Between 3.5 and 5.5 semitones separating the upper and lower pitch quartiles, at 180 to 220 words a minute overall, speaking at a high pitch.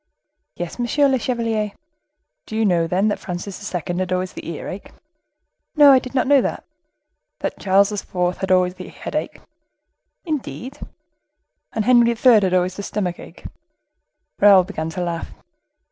No: average, 4.6 semitones; average, 155 wpm; high, 200 Hz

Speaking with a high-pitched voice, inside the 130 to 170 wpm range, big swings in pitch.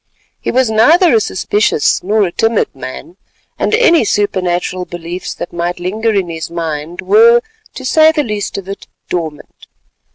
Yes: high, 200 Hz; average, 160 wpm; wide, 5.7 semitones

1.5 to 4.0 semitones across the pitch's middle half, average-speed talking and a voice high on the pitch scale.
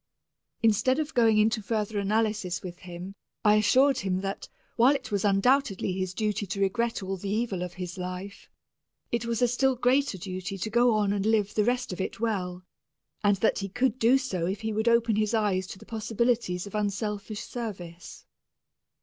Yes: average, 3.5 semitones; average, 190 wpm; high, 210 Hz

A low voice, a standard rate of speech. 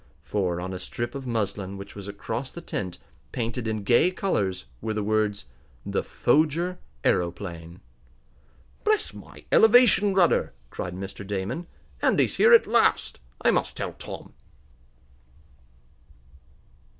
No: low, 110 Hz; slow, 125 wpm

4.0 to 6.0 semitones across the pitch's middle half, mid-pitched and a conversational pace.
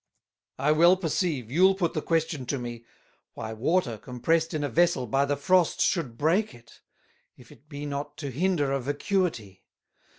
Yes: average, 5.1 semitones; medium, 145 Hz; average, 170 wpm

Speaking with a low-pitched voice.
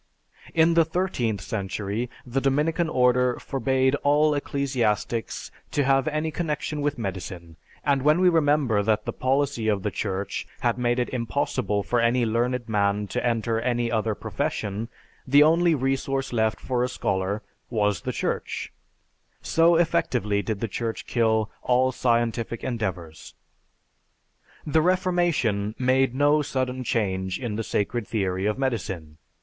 Yes: low, 120 Hz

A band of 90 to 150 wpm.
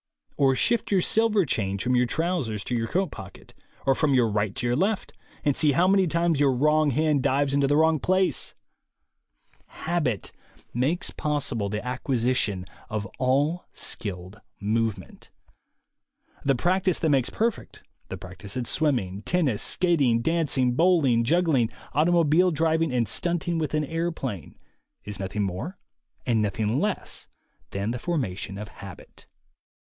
Yes: average, 145 wpm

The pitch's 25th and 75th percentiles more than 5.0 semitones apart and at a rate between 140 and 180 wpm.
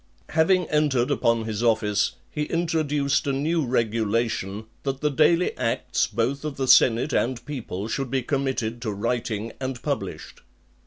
No: average, 4.3 semitones; average, 155 wpm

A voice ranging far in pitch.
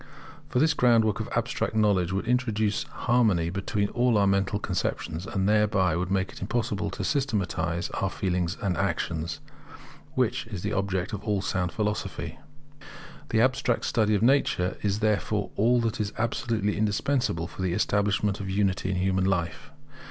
No: average, 2.9 semitones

